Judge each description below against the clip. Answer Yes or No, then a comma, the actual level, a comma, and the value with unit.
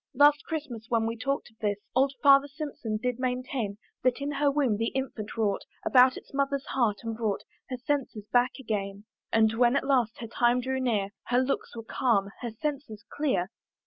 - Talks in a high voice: Yes, high, 245 Hz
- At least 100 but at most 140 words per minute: No, average, 190 wpm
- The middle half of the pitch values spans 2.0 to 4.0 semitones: Yes, average, 3.7 semitones